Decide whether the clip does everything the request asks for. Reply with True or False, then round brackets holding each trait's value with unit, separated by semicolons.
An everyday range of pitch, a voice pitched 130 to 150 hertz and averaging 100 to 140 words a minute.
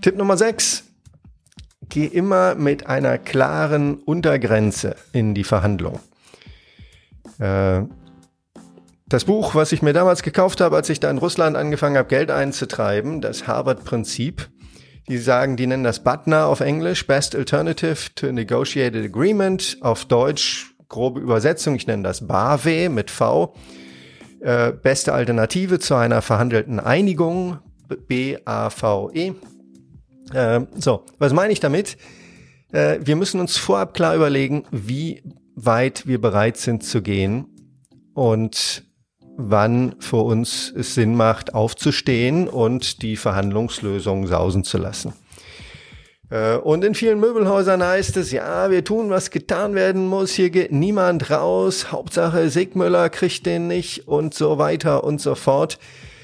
False (7.2 semitones; 135 Hz; 130 wpm)